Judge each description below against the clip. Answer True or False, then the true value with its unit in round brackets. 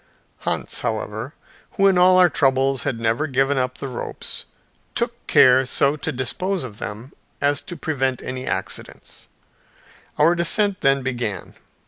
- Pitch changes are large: False (3.9 semitones)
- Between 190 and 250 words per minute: False (145 wpm)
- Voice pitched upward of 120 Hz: True (135 Hz)